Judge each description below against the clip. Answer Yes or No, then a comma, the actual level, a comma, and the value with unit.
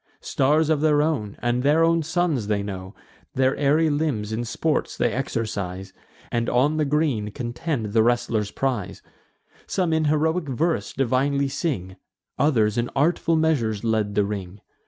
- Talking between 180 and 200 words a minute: No, average, 155 wpm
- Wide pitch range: Yes, wide, 6.2 semitones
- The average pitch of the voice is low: Yes, low, 130 Hz